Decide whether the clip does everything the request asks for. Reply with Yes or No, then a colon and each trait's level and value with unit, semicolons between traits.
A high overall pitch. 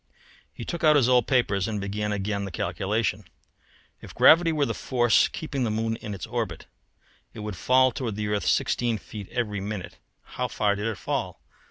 No: low, 105 Hz